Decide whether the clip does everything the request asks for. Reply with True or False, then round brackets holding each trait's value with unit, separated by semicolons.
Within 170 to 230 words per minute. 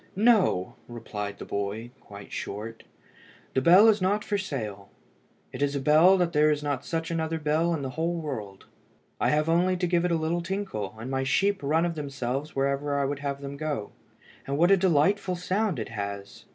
True (200 wpm)